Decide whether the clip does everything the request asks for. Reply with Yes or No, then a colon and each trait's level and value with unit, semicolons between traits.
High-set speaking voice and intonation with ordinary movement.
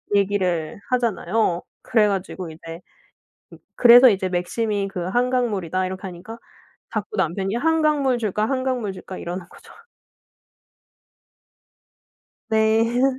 Yes: high, 210 Hz; average, 4.5 semitones